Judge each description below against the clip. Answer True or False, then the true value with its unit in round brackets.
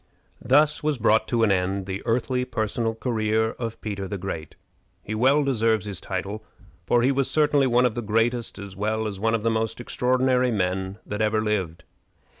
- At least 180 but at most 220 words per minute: True (190 wpm)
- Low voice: True (110 Hz)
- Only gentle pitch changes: False (3.4 semitones)